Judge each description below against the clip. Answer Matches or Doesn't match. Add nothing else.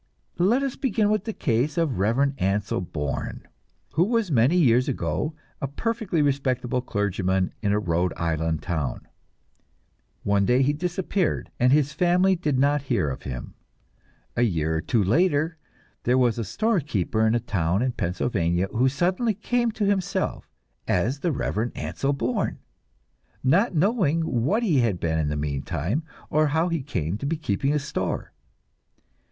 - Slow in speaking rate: Doesn't match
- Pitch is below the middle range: Matches